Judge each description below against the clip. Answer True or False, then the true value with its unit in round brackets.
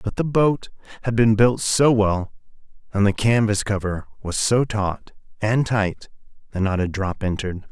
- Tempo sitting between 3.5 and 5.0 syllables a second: True (4.5 syllables/s)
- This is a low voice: True (105 Hz)